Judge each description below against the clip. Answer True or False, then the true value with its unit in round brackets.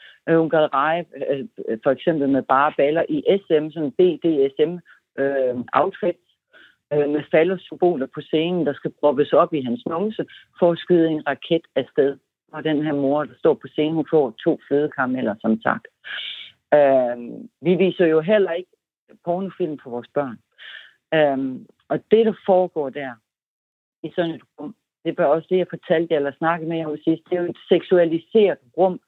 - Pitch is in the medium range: True (160 Hz)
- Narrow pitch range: False (3.6 semitones)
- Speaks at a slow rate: False (170 wpm)